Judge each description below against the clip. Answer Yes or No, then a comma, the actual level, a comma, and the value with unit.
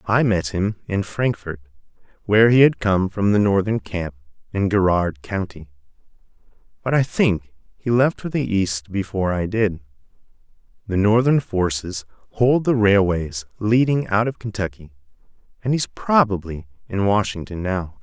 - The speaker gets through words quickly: No, average, 145 wpm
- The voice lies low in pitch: Yes, low, 100 Hz